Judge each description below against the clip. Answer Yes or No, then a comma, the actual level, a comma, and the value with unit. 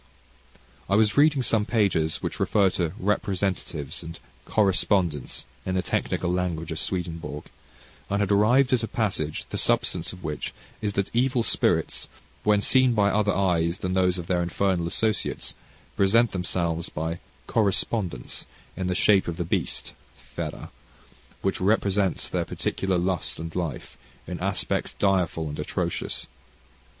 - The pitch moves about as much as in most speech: Yes, average, 3.4 semitones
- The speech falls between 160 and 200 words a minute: No, average, 145 wpm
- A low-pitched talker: Yes, very low, 95 Hz